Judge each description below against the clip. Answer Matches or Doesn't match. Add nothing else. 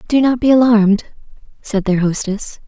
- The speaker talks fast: Doesn't match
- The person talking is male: Doesn't match